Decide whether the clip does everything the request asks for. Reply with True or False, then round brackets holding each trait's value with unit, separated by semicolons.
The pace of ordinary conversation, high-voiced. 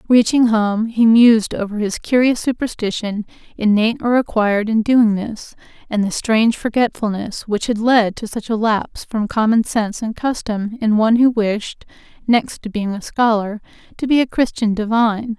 True (170 wpm; 220 Hz)